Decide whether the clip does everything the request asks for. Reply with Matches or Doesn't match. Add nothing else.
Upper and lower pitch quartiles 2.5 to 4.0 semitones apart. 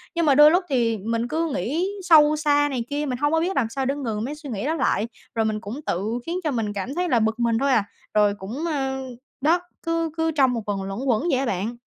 Doesn't match